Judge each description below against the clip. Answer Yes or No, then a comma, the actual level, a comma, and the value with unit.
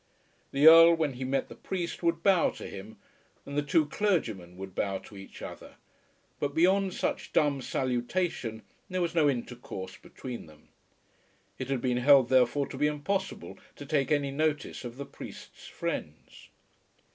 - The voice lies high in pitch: No, medium, 140 Hz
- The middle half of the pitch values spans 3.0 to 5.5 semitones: Yes, average, 5.0 semitones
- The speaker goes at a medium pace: Yes, average, 165 wpm